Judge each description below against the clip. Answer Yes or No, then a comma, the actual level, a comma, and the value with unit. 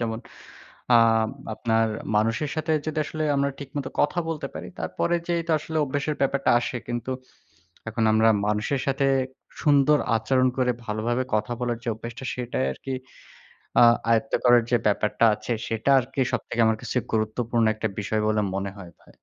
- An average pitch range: Yes, average, 3.7 semitones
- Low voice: Yes, low, 120 Hz